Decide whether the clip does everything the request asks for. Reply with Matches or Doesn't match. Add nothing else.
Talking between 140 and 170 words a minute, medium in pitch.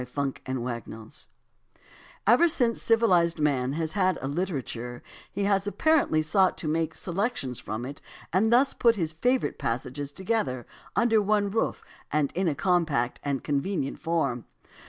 Matches